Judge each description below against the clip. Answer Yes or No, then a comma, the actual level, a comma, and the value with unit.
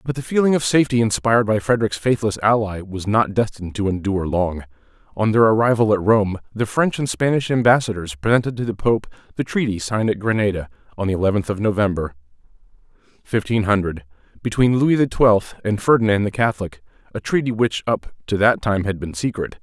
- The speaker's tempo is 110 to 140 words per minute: No, average, 185 wpm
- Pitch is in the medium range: No, low, 105 Hz